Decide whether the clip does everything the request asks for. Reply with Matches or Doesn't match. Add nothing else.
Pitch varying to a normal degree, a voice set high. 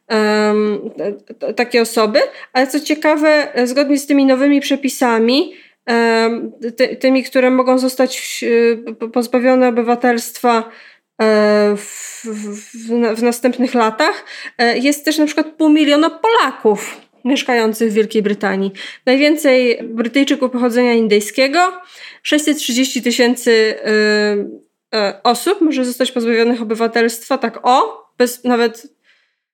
Matches